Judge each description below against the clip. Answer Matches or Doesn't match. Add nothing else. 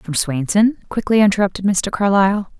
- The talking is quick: Doesn't match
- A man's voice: Doesn't match